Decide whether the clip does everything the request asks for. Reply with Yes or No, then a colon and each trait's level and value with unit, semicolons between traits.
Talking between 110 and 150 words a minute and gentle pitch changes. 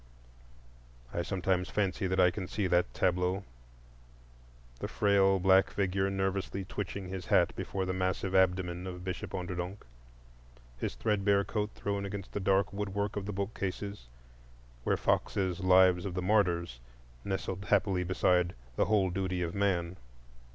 Yes: average, 140 wpm; narrow, 1.5 semitones